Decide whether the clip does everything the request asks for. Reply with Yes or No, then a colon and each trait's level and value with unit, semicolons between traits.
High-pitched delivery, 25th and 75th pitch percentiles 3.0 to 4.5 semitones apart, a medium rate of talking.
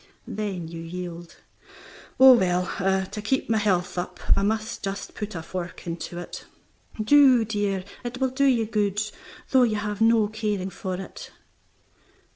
Yes: high, 205 Hz; average, 3.6 semitones; average, 155 wpm